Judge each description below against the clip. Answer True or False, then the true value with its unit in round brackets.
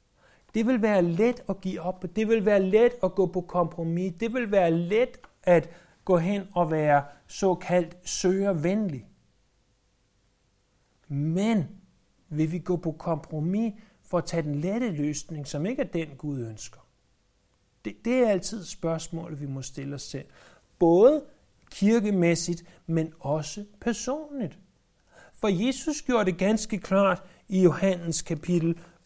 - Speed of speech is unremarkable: False (140 wpm)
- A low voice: False (175 Hz)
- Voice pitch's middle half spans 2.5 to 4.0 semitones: False (4.8 semitones)